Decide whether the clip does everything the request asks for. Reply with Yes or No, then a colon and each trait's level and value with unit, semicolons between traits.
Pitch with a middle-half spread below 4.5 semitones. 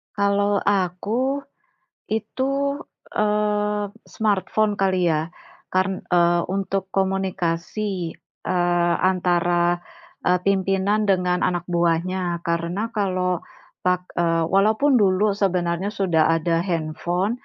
Yes: average, 2.9 semitones